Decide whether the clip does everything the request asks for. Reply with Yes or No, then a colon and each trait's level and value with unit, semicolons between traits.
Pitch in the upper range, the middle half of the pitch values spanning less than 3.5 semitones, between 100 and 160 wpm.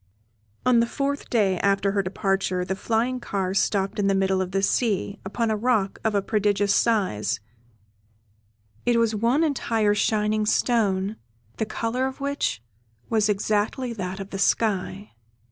Yes: high, 210 Hz; average, 3.0 semitones; average, 155 wpm